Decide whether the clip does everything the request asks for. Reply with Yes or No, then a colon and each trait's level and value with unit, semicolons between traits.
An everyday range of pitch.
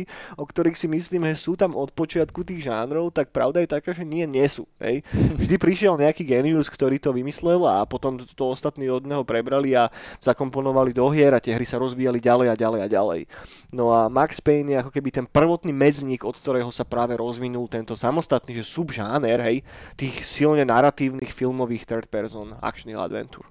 Yes: average, 4.2 semitones